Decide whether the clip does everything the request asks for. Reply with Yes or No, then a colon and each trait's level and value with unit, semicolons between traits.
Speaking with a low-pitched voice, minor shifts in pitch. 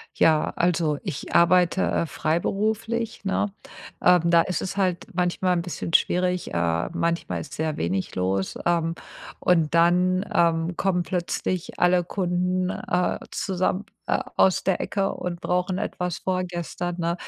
No: medium, 175 Hz; narrow, 1.6 semitones